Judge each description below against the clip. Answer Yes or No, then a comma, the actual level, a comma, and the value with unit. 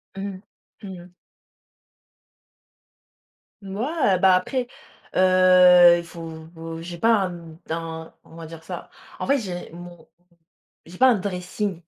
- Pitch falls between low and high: Yes, medium, 180 Hz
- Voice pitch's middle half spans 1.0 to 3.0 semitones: Yes, average, 2.7 semitones